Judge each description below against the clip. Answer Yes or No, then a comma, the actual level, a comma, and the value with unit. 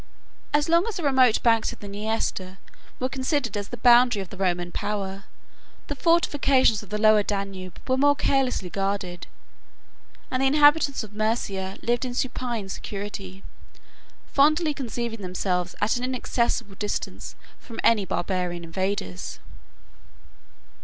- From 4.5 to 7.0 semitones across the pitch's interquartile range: Yes, average, 5.0 semitones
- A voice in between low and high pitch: No, high, 215 Hz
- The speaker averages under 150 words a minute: Yes, average, 140 wpm